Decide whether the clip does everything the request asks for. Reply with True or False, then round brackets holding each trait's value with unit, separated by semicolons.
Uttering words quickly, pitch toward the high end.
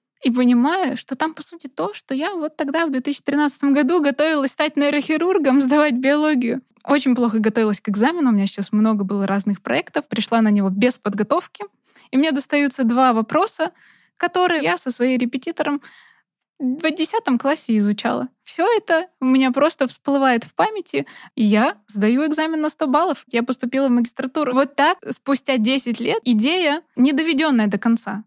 True (170 wpm; 270 Hz)